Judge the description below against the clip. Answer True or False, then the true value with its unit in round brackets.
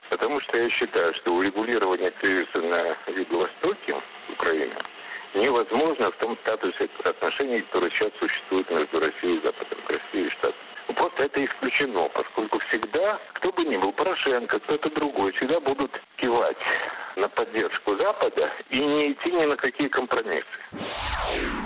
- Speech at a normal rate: True (140 wpm)